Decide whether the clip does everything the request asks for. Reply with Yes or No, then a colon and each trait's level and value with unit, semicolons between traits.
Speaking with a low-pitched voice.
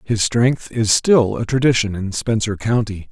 Yes: low, 110 Hz